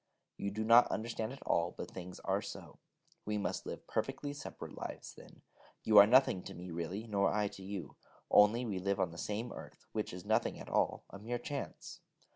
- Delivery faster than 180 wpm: Yes, fast, 205 wpm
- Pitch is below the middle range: Yes, low, 105 Hz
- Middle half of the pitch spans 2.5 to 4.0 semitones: Yes, average, 3.4 semitones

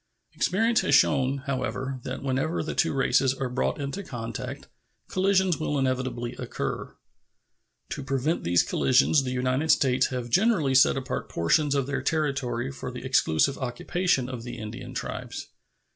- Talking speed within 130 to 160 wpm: Yes, average, 150 wpm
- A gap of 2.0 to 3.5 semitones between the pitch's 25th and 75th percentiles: Yes, average, 2.7 semitones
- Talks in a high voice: No, low, 135 Hz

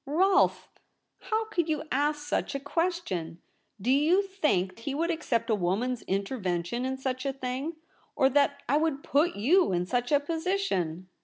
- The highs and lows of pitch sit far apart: Yes, wide, 6.1 semitones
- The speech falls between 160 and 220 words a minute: Yes, average, 175 wpm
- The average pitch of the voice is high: Yes, very high, 275 Hz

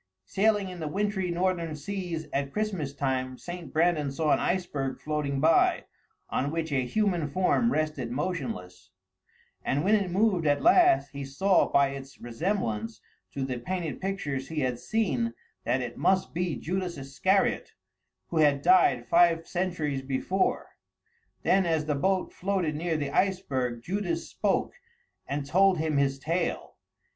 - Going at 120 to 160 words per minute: Yes, average, 150 wpm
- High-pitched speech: No, medium, 160 Hz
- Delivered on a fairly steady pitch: No, average, 5.2 semitones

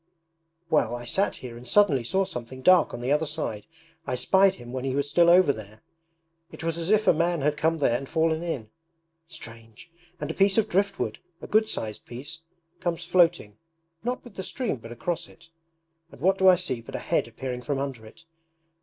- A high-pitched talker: No, medium, 155 Hz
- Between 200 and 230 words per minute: Yes, fast, 205 wpm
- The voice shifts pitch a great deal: Yes, wide, 6.5 semitones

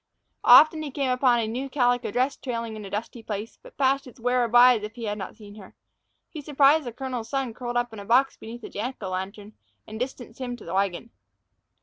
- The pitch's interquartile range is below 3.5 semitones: Yes, average, 3.1 semitones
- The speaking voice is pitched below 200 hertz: No, high, 240 Hz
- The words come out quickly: Yes, fast, 235 wpm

